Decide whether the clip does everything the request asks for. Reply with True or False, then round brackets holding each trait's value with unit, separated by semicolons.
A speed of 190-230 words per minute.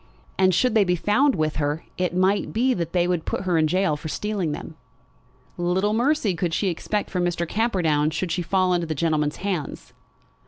True (200 wpm)